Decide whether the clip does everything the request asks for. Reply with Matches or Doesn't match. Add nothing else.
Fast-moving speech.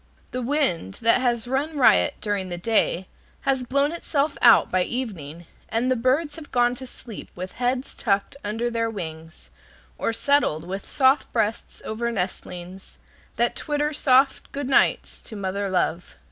Doesn't match